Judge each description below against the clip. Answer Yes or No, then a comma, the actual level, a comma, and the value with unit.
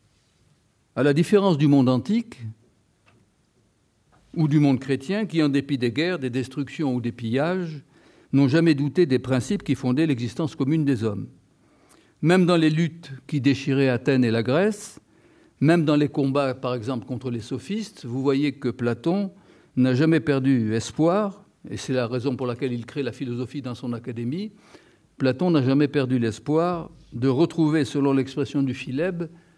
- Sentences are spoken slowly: No, average, 165 wpm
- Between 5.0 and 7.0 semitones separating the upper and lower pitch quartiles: No, average, 4.3 semitones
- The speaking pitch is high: No, medium, 140 Hz